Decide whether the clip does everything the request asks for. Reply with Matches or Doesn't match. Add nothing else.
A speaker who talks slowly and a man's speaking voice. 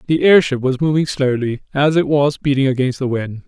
Doesn't match